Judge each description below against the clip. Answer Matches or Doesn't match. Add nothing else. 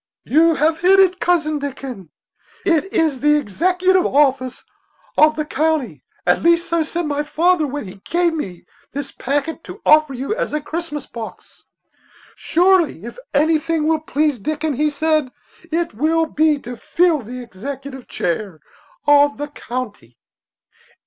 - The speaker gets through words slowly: Doesn't match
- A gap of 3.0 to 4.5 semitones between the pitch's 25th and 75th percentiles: Matches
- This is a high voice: Matches